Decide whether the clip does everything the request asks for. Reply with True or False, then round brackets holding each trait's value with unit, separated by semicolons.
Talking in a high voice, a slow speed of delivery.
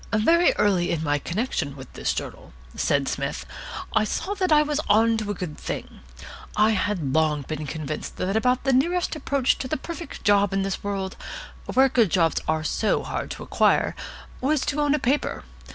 False (210 Hz; 190 wpm)